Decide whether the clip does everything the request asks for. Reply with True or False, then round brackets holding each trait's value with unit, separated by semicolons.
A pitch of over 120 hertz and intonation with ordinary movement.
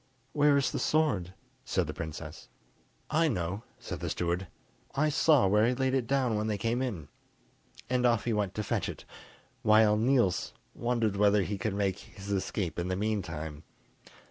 False (105 Hz; 4.8 semitones)